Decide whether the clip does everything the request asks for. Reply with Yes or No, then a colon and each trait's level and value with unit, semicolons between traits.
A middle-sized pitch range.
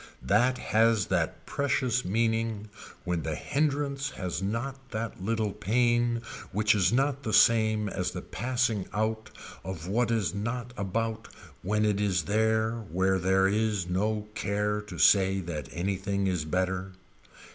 Yes: average, 3.3 semitones